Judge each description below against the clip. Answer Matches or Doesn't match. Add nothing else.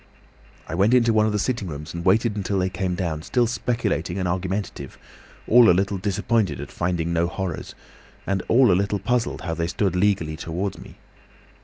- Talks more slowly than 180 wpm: Doesn't match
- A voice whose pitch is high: Doesn't match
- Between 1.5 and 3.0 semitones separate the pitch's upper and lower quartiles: Doesn't match